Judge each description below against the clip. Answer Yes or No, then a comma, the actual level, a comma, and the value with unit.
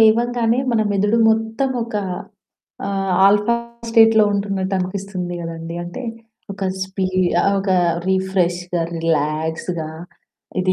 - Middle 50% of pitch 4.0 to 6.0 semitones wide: No, average, 3.6 semitones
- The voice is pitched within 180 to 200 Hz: Yes, high, 195 Hz